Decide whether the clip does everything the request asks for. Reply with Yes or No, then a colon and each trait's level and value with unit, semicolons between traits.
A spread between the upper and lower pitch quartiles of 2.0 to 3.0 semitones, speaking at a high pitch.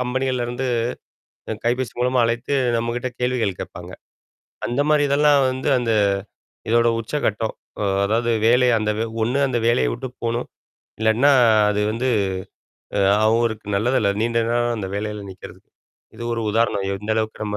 No: narrow, 2.5 semitones; low, 115 Hz